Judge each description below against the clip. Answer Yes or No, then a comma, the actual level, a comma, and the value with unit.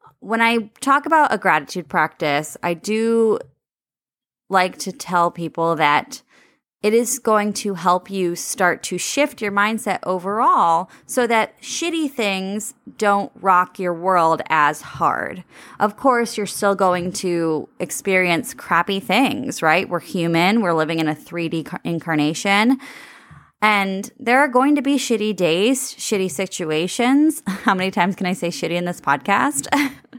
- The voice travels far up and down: Yes, wide, 5.8 semitones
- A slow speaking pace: No, average, 150 wpm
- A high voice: Yes, high, 200 Hz